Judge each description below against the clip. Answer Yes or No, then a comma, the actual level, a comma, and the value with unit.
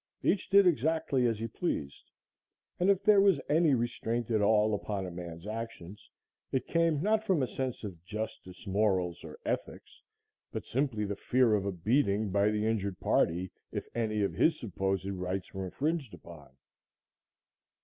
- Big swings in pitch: Yes, wide, 6.2 semitones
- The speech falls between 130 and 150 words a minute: No, average, 165 wpm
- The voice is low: Yes, low, 110 Hz